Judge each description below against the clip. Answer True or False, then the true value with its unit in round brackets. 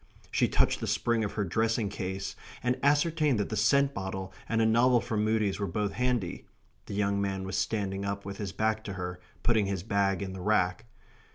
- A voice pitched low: True (105 Hz)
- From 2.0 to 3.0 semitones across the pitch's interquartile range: True (2.7 semitones)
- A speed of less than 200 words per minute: False (205 wpm)